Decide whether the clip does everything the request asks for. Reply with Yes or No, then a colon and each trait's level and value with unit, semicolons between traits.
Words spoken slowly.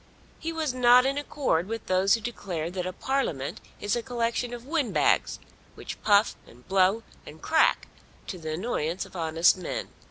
No: average, 170 wpm